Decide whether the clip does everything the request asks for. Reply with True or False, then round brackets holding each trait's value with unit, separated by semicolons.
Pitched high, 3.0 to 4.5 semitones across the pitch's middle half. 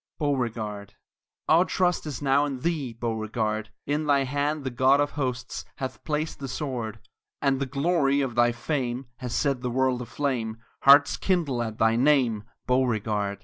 False (130 Hz; 3.5 semitones)